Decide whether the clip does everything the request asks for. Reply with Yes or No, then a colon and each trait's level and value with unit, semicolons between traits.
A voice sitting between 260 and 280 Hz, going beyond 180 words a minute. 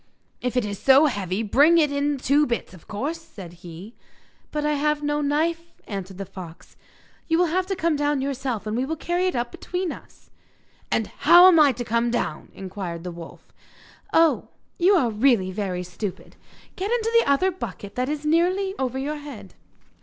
Yes: very high, 275 Hz; average, 190 wpm